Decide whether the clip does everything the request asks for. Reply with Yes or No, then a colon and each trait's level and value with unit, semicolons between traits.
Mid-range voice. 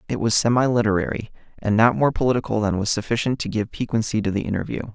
No: low, 110 Hz